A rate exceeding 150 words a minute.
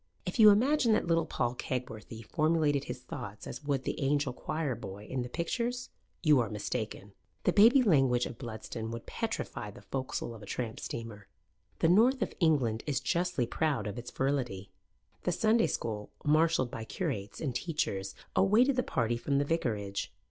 Yes: average, 175 wpm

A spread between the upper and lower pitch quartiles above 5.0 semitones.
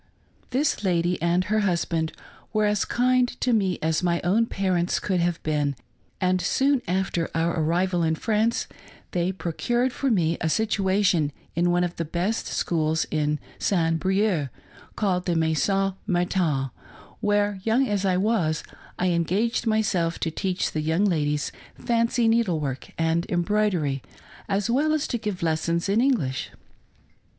No: average, 4.3 semitones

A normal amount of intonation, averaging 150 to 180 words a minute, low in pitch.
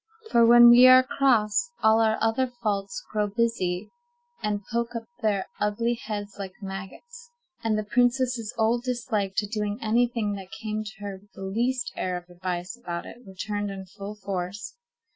No: average, 3.2 semitones; average, 175 wpm; high, 215 Hz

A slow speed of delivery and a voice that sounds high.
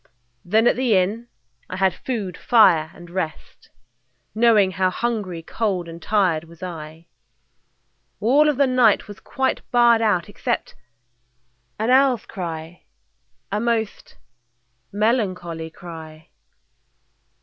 Yes: slow, 115 wpm; high, 200 Hz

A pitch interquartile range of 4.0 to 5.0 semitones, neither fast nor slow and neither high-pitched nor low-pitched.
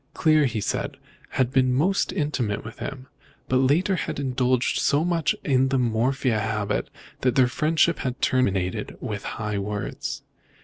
No: average, 4.4 semitones; average, 160 wpm; low, 130 Hz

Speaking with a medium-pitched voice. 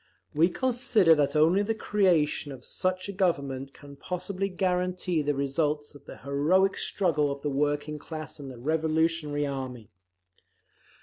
Yes: medium, 155 Hz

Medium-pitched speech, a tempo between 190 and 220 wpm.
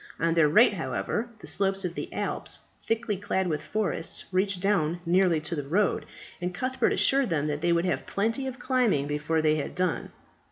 Yes: medium, 180 Hz; average, 195 wpm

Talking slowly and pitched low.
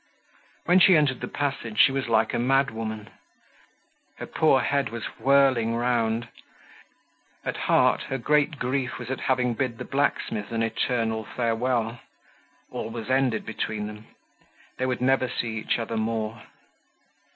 No: average, 150 wpm; low, 120 Hz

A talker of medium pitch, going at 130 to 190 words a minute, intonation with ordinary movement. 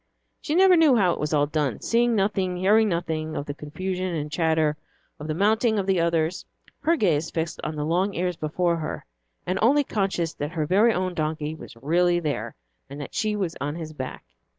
No: medium, 170 Hz; fast, 205 wpm; average, 4.3 semitones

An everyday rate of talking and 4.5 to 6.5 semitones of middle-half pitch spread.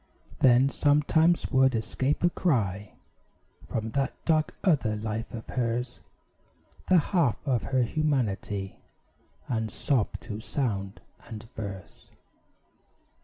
No: slow, 110 wpm; average, 4.8 semitones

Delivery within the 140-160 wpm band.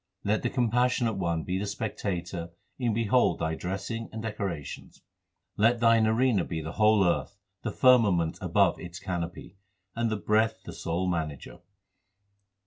Yes: average, 145 wpm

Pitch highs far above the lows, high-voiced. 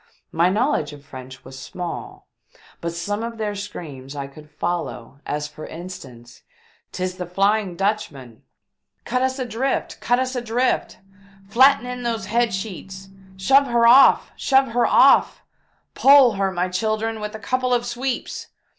Yes: wide, 6.0 semitones; high, 205 Hz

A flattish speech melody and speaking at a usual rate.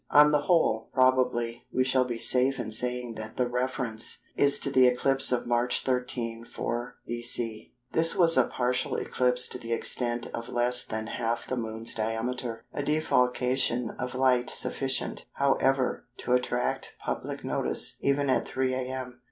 Yes: narrow, 1.7 semitones; average, 160 wpm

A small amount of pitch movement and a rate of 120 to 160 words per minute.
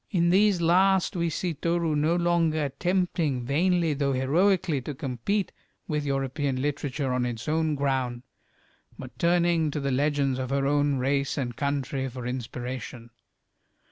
No: average, 4.3 semitones; average, 145 wpm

